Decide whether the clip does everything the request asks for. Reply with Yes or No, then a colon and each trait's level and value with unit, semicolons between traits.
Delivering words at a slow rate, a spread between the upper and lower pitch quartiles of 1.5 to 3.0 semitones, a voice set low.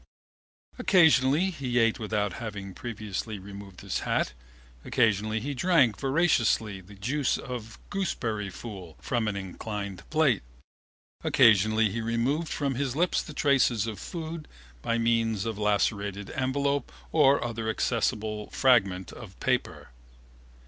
No: slow, 130 wpm; average, 4.8 semitones; low, 115 Hz